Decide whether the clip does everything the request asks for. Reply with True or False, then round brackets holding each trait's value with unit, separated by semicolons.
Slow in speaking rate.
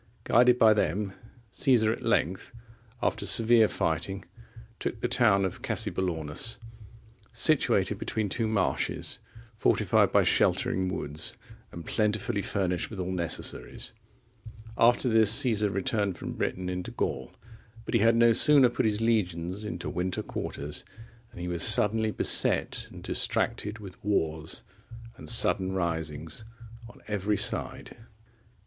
True (130 wpm)